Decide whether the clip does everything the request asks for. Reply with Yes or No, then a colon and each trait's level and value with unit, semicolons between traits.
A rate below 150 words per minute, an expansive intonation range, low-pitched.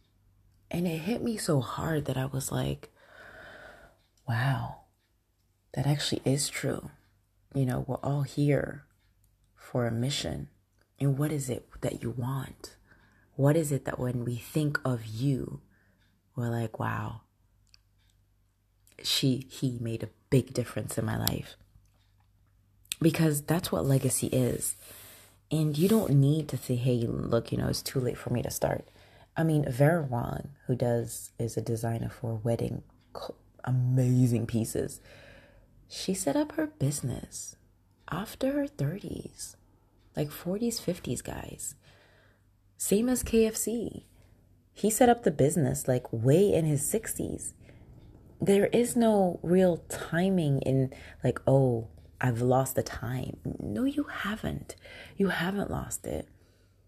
Yes: average, 140 wpm; wide, 6.4 semitones; low, 125 Hz